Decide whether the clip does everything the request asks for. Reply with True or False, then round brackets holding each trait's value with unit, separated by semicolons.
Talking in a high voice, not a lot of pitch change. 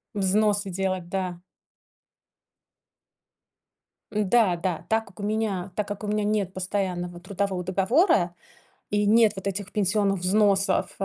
True (195 Hz; 2.2 semitones)